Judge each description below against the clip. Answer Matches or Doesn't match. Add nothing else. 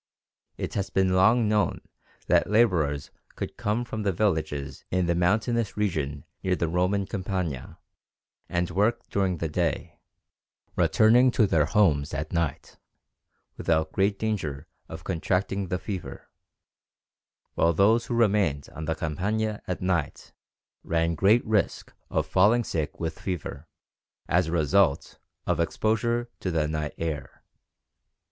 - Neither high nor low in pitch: Doesn't match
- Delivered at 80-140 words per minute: Matches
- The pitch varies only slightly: Doesn't match